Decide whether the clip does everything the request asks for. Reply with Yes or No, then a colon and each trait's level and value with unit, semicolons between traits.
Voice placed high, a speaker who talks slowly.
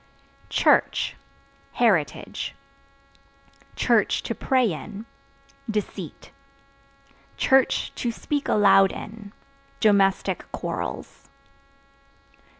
Yes: high, 210 Hz; slow, 55 wpm